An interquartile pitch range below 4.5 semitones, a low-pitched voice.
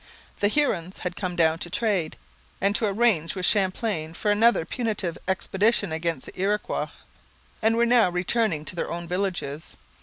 No: average, 4.1 semitones; high, 190 Hz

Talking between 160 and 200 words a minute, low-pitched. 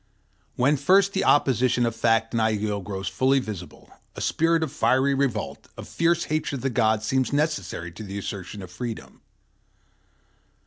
Yes: average, 165 wpm; low, 120 Hz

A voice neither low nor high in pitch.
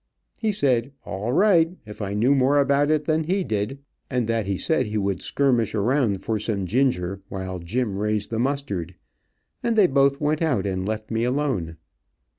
No: low, 120 Hz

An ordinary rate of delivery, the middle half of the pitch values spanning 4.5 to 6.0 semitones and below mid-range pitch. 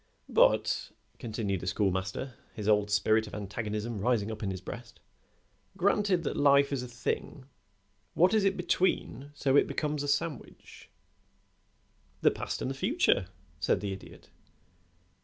Yes: average, 150 wpm; wide, 5.6 semitones; low, 120 Hz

